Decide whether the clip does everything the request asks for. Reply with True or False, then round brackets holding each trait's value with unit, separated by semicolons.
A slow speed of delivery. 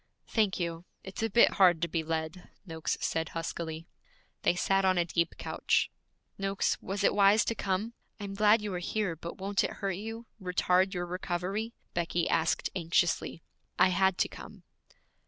False (175 wpm)